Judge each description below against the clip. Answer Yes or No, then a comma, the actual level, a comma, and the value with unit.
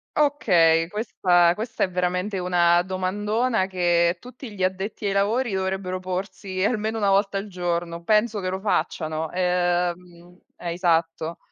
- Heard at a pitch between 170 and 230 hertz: Yes, medium, 185 Hz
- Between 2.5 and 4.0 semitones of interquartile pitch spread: Yes, average, 2.8 semitones